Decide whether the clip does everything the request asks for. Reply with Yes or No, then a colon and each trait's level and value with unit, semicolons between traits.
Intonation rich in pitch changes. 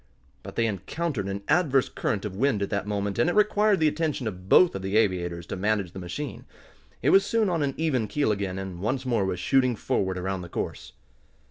Yes: wide, 7.4 semitones